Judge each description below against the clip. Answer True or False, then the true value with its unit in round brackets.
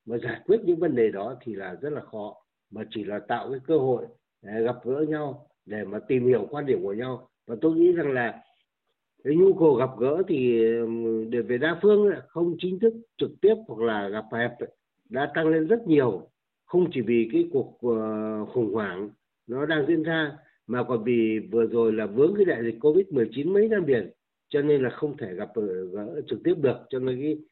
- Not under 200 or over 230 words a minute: True (220 wpm)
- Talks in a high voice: False (150 Hz)